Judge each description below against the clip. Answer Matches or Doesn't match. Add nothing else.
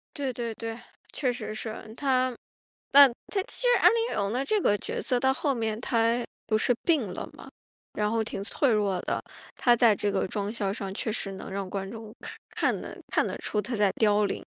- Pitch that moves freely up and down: Doesn't match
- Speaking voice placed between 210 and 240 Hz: Matches